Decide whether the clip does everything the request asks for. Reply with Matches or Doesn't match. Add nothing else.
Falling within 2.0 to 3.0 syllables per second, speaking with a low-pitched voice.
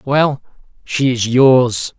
Matches